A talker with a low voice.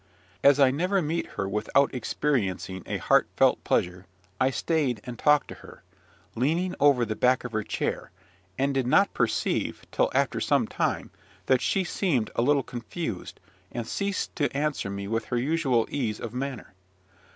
Yes: low, 130 Hz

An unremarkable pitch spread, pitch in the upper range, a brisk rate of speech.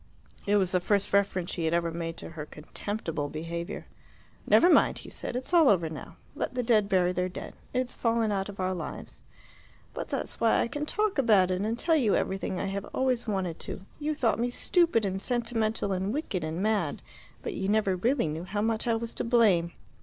Yes: average, 4.4 semitones; high, 205 Hz; fast, 215 wpm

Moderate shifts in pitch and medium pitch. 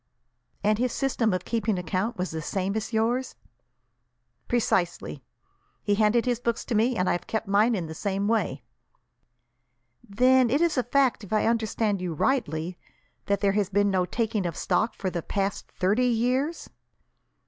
No: average, 3.9 semitones; high, 215 Hz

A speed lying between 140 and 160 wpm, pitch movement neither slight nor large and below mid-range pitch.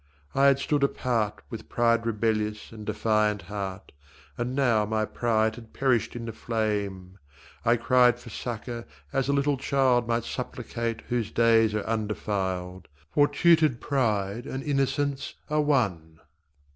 Yes: average, 145 wpm; average, 3.5 semitones; low, 115 Hz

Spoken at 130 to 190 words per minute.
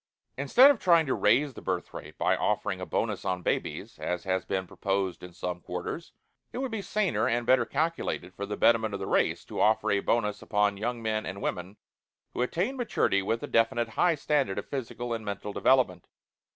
No: fast, 205 wpm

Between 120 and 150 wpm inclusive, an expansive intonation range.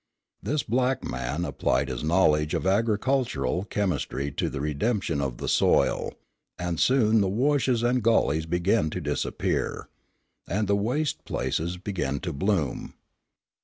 Yes: slow, 135 wpm; wide, 7.1 semitones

